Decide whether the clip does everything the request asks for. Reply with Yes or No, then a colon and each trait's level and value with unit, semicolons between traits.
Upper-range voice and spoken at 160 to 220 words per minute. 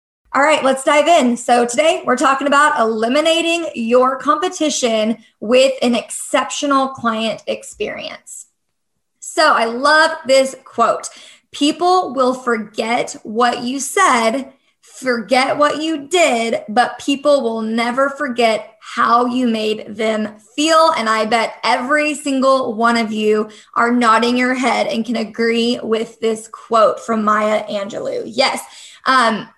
No: very high, 250 Hz; slow, 135 wpm